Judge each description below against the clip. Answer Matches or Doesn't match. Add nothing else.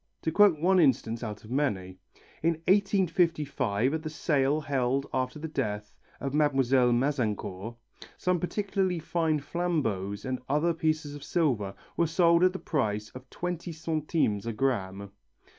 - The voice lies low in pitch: Doesn't match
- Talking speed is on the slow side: Doesn't match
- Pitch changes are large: Matches